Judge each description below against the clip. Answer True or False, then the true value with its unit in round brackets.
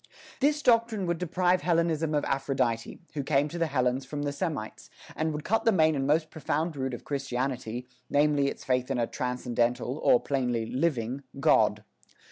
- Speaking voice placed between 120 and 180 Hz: True (140 Hz)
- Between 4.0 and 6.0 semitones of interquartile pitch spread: True (4.5 semitones)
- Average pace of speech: True (175 wpm)